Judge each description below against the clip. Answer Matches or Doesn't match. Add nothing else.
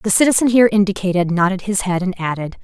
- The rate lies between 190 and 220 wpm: Matches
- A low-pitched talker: Doesn't match